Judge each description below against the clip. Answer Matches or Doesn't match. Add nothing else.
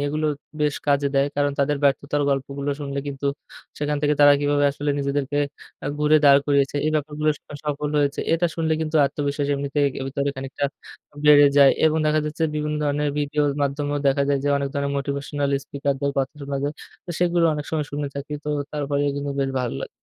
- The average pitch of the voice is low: Doesn't match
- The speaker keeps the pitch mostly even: Matches